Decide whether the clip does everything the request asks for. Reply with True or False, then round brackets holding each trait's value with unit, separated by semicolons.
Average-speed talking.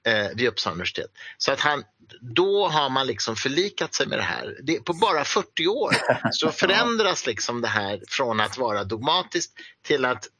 True (180 wpm)